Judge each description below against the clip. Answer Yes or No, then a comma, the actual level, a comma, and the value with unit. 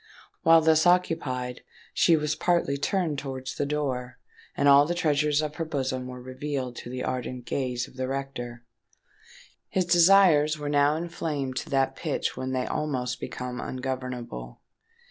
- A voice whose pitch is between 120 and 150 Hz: Yes, medium, 140 Hz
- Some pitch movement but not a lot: Yes, average, 3.3 semitones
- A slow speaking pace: No, average, 155 wpm